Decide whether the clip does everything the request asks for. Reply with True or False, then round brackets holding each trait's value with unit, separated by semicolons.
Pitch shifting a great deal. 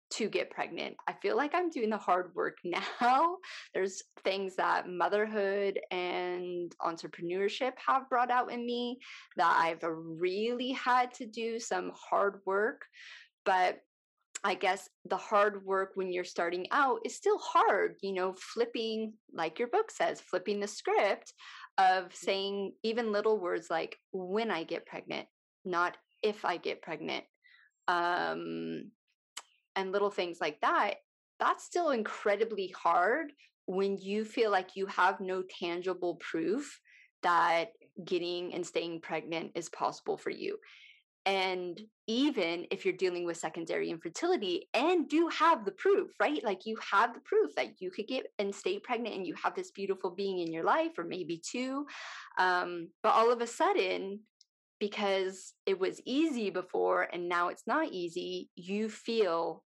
True (6.3 semitones)